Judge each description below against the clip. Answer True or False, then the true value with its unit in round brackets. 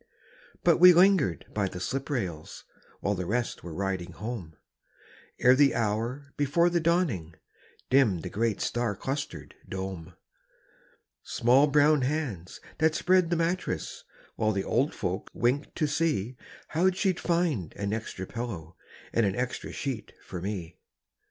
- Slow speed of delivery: False (145 wpm)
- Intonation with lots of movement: True (7.9 semitones)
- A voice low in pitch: True (120 Hz)